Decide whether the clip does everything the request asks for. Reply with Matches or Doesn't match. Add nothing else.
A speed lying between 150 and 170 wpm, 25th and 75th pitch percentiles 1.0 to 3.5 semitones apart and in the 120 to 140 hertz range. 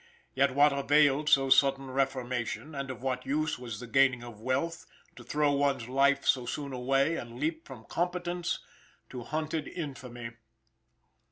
Matches